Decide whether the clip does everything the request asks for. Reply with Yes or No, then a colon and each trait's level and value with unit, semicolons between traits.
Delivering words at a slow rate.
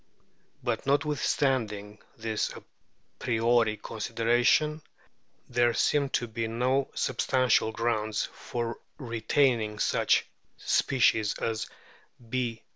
Yes: slow, 95 wpm